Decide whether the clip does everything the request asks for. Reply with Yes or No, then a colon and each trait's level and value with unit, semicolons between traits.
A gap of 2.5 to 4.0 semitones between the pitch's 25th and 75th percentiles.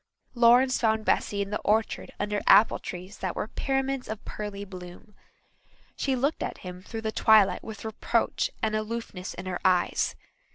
Yes: average, 2.9 semitones